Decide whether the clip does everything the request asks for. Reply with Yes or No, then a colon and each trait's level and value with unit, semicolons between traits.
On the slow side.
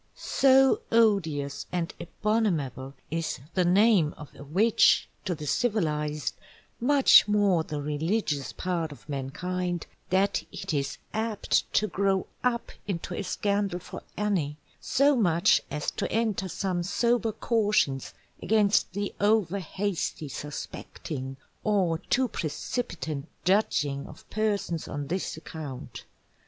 Yes: slow, 120 wpm